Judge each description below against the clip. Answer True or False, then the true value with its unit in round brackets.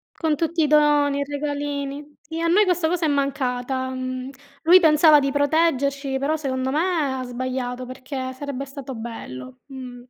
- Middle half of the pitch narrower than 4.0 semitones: True (2.7 semitones)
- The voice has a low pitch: False (280 Hz)